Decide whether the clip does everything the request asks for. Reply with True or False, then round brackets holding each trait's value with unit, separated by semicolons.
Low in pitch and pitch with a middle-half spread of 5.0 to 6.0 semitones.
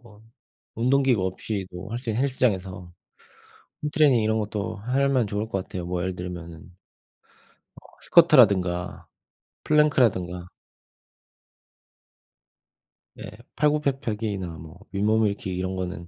True (105 Hz; 5.4 semitones)